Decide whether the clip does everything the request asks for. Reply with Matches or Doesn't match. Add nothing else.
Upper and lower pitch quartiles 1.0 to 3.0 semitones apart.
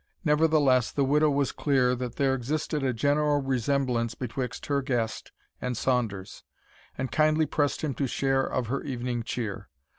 Matches